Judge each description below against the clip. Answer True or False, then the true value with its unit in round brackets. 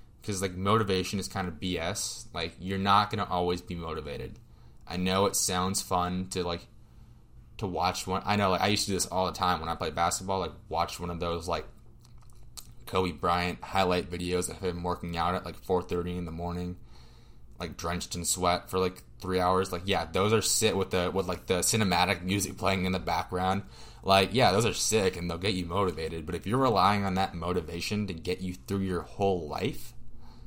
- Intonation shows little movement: True (2.0 semitones)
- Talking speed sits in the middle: False (215 wpm)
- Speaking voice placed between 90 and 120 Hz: True (95 Hz)